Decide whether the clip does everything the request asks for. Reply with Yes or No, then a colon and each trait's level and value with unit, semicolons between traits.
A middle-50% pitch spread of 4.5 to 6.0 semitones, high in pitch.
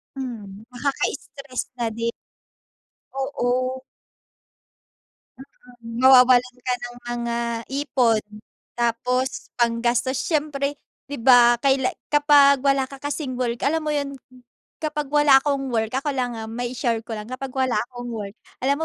No: average, 2.7 semitones; very high, 255 Hz